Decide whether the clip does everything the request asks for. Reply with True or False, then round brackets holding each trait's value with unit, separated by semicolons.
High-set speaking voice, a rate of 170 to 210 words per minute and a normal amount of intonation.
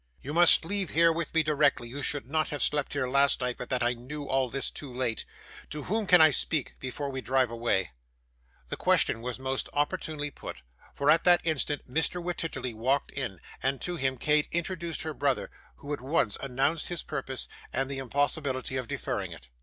False (140 Hz; 200 wpm; 3.4 semitones)